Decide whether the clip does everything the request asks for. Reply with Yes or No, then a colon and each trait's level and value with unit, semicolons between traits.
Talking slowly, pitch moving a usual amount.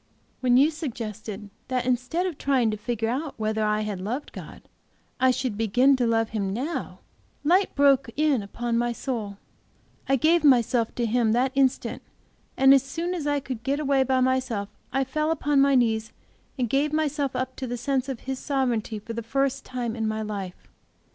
No: average, 190 wpm; average, 3.5 semitones